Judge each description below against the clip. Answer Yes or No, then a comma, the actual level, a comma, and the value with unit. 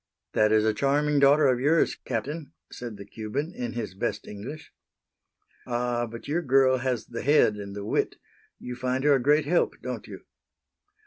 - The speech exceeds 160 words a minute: Yes, average, 180 wpm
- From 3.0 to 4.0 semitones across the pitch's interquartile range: No, average, 4.6 semitones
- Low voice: Yes, low, 125 Hz